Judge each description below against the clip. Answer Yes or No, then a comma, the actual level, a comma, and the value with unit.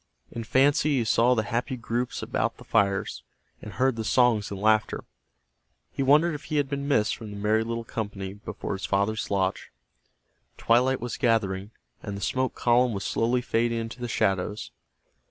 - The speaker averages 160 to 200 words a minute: Yes, average, 175 wpm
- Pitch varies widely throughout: No, average, 3.5 semitones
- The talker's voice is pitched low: Yes, low, 115 Hz